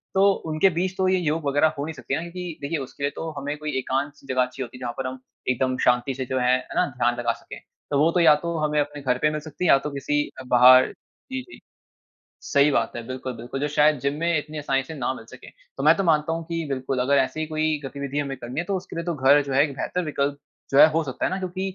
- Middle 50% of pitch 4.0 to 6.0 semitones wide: No, average, 3.6 semitones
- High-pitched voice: No, medium, 145 Hz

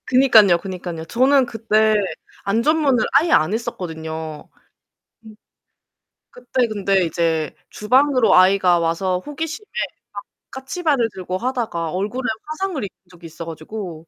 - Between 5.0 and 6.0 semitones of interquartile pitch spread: No, wide, 7.1 semitones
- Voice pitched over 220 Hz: No, high, 210 Hz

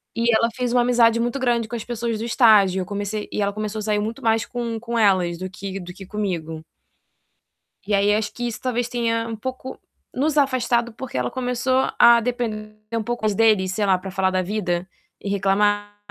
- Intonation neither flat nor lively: Yes, average, 3.0 semitones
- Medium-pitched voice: No, high, 220 Hz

